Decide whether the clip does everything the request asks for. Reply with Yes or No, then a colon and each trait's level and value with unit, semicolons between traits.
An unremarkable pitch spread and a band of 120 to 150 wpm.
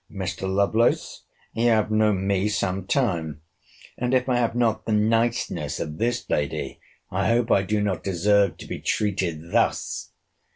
No: average, 3.3 semitones; average, 160 wpm